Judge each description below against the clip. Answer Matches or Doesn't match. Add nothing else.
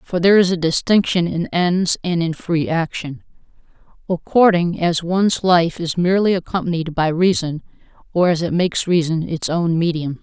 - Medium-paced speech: Matches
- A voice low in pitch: Doesn't match